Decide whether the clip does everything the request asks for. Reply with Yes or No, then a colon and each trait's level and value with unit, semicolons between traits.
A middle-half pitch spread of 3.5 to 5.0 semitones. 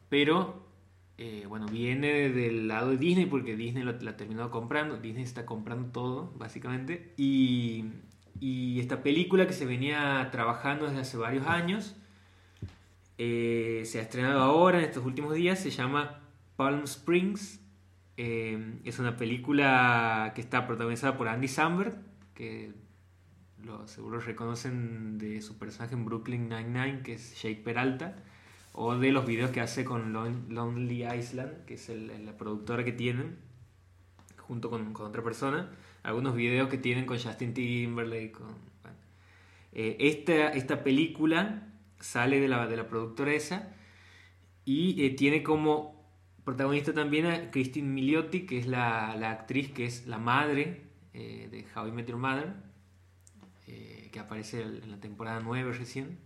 Yes: average, 3.8 semitones